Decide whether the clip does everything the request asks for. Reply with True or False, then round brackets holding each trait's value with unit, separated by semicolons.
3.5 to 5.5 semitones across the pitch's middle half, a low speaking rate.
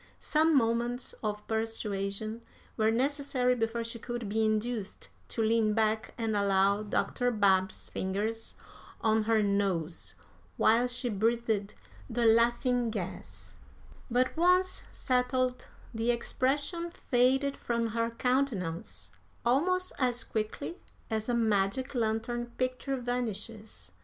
False (2.7 semitones; 115 wpm)